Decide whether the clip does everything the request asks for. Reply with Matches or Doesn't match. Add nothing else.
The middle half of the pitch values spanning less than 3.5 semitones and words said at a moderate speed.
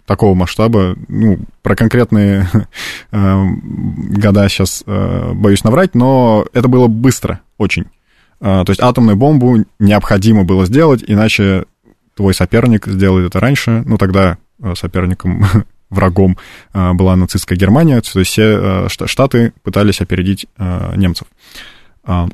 Matches